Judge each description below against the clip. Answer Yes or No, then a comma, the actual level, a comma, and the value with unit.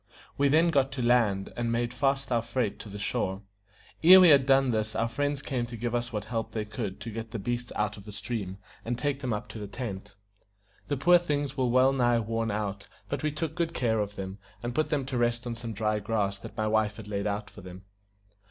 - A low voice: Yes, low, 115 Hz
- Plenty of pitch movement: No, average, 4.2 semitones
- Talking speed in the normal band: No, fast, 245 wpm